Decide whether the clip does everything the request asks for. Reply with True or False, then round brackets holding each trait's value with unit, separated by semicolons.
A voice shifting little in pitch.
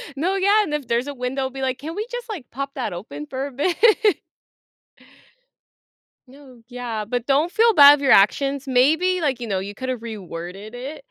False (4.1 semitones)